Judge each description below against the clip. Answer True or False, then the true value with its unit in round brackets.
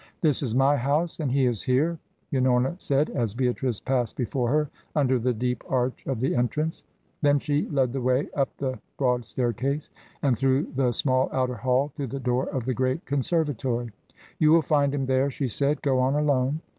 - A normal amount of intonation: False (2.2 semitones)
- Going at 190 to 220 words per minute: True (195 wpm)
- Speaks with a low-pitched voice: True (130 Hz)